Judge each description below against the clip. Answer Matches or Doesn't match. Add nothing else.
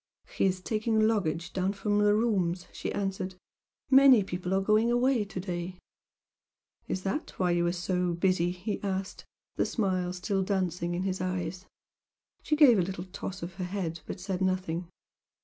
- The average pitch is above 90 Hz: Matches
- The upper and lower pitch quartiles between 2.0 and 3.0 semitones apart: Matches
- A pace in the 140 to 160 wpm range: Doesn't match